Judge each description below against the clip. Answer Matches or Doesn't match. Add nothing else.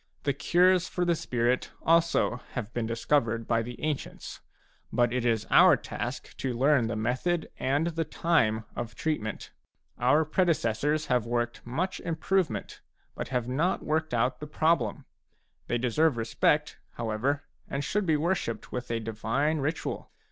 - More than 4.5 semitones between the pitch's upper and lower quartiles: Matches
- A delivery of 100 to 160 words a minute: Matches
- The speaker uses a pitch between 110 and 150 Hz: Matches